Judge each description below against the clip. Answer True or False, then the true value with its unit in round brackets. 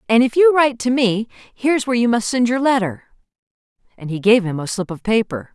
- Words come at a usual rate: False (225 wpm)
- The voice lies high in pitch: True (230 Hz)